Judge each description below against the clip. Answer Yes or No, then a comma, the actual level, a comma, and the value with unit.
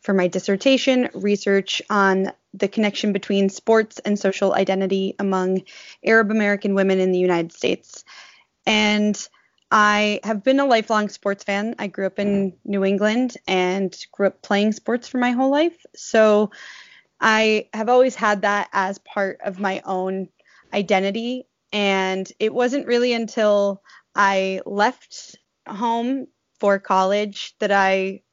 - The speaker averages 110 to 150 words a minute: Yes, average, 140 wpm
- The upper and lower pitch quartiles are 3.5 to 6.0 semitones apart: No, narrow, 2.4 semitones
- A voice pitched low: No, high, 205 Hz